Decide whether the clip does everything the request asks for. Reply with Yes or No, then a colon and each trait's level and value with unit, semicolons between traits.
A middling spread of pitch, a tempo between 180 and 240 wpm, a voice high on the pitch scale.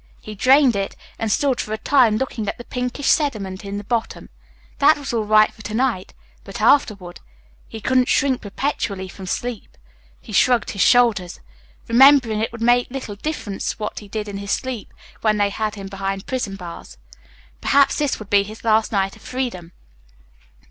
Yes: average, 4.1 semitones; average, 185 wpm; high, 220 Hz